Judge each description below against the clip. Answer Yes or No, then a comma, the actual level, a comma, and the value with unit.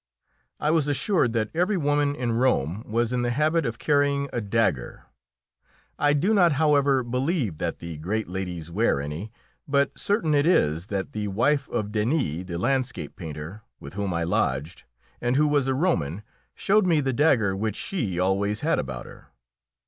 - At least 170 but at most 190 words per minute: Yes, average, 175 wpm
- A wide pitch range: Yes, wide, 7.3 semitones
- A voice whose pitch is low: Yes, low, 120 Hz